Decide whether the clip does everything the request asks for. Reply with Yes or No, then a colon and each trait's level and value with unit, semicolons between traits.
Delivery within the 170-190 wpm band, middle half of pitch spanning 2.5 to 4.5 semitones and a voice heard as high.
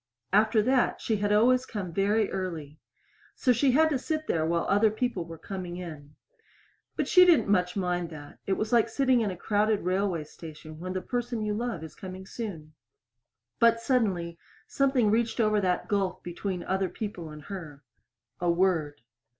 No: average, 175 wpm; average, 4.9 semitones; high, 195 Hz